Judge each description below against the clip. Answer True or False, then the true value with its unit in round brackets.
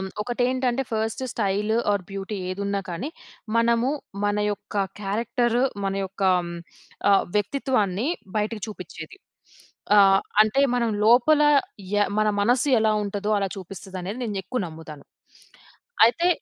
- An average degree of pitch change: True (3.5 semitones)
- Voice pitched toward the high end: True (210 Hz)